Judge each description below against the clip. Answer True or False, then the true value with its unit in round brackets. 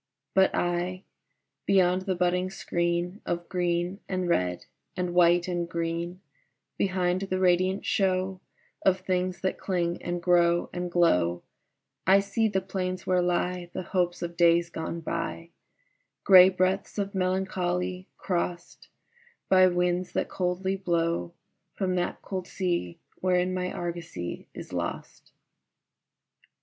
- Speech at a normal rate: False (130 wpm)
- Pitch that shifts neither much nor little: False (1.3 semitones)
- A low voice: False (180 Hz)